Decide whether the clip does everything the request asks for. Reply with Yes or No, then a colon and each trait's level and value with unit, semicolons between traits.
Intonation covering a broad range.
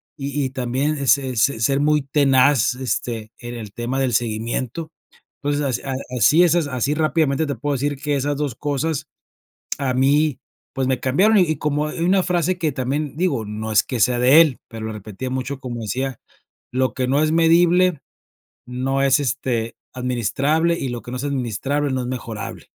No: average, 3.1 semitones